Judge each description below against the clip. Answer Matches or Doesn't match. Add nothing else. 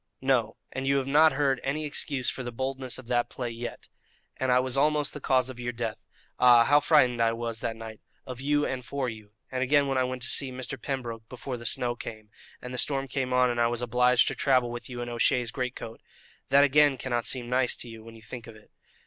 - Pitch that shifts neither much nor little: Doesn't match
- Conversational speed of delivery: Doesn't match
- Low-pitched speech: Matches